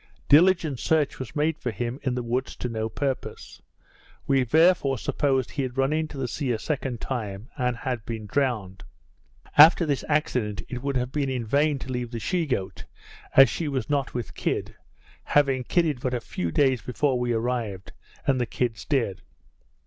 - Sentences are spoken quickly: No, average, 185 wpm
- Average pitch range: Yes, average, 3.3 semitones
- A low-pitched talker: Yes, low, 130 Hz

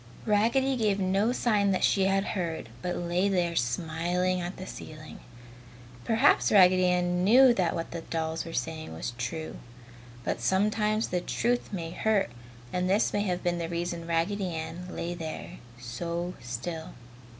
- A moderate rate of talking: Yes, average, 160 wpm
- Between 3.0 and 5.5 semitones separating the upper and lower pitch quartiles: Yes, average, 3.3 semitones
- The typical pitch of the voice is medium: Yes, medium, 180 Hz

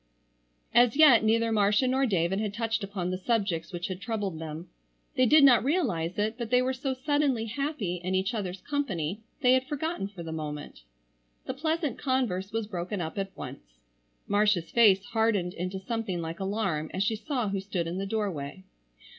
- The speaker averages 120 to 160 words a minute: No, average, 185 wpm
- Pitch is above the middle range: Yes, high, 205 Hz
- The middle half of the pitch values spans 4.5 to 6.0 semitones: Yes, average, 5.2 semitones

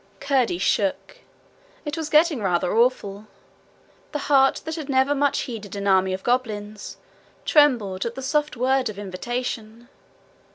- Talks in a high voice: Yes, high, 240 Hz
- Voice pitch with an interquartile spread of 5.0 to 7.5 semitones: Yes, average, 5.3 semitones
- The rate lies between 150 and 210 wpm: No, average, 140 wpm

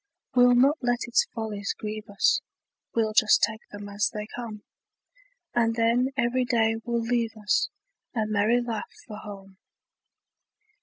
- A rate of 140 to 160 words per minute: Yes, average, 145 wpm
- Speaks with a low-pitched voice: No, high, 225 Hz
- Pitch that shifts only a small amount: Yes, narrow, 2.2 semitones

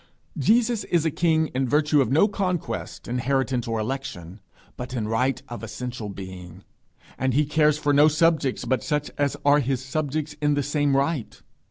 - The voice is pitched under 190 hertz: Yes, medium, 140 Hz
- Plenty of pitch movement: No, average, 3.6 semitones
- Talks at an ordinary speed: Yes, average, 175 wpm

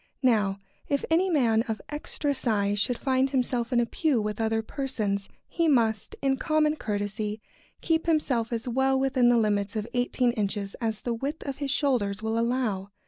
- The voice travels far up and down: No, average, 4.1 semitones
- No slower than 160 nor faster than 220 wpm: Yes, average, 180 wpm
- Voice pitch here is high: Yes, high, 240 Hz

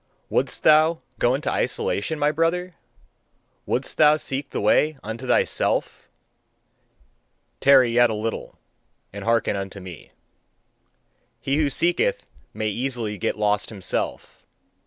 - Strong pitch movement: Yes, wide, 6.2 semitones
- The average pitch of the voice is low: Yes, low, 130 Hz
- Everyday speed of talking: No, slow, 120 wpm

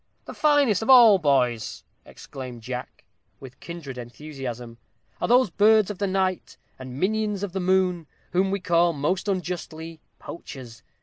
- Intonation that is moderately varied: No, wide, 6.8 semitones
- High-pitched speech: No, medium, 175 Hz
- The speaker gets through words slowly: No, average, 150 wpm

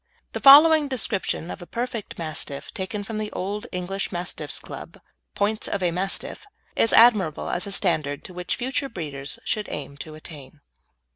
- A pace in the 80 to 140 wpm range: No, average, 165 wpm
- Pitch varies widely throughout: Yes, wide, 5.7 semitones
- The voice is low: No, high, 190 Hz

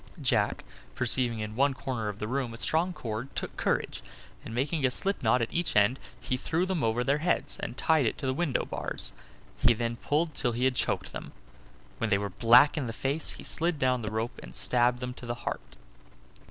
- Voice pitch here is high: No, low, 125 Hz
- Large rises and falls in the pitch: No, average, 3.8 semitones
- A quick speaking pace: Yes, fast, 220 wpm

